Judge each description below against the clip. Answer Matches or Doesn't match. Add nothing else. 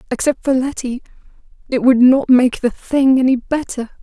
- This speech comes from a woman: Matches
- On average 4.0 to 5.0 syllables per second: Matches